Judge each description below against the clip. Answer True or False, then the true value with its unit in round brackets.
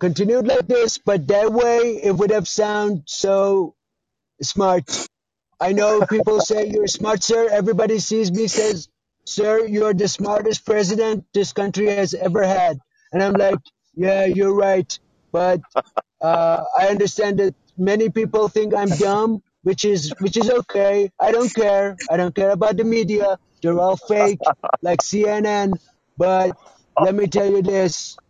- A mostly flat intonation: True (2.3 semitones)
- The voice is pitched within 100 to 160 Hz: False (200 Hz)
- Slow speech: False (155 wpm)